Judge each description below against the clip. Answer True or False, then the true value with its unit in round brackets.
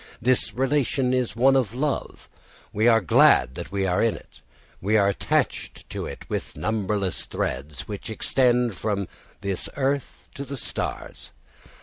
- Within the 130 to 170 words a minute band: True (150 wpm)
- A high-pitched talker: False (110 Hz)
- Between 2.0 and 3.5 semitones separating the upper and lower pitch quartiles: False (4.5 semitones)